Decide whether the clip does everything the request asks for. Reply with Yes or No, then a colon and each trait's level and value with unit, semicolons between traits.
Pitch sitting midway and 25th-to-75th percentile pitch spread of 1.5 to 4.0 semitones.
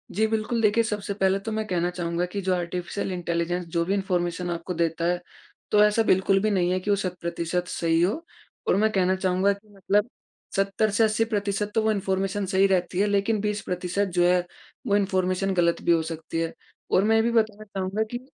No: high, 195 Hz; average, 2.7 semitones